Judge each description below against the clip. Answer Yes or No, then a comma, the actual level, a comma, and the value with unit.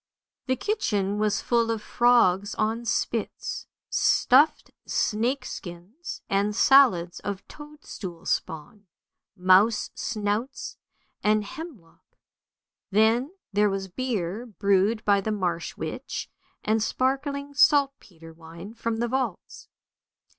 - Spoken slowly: Yes, slow, 110 wpm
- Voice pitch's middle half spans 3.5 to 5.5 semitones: Yes, average, 4.8 semitones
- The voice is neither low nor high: No, high, 215 Hz